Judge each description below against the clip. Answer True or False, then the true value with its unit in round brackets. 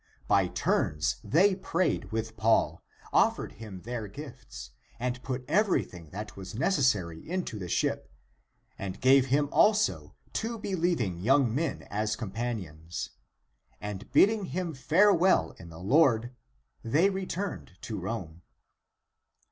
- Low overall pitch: True (120 Hz)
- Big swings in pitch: True (8.8 semitones)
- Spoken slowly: True (125 wpm)